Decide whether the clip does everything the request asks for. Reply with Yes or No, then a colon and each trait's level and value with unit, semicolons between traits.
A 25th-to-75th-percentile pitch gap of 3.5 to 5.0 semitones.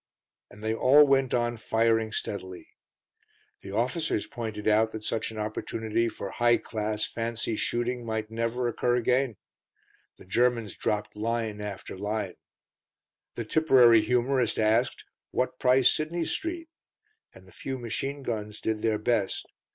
No: narrow, 2.6 semitones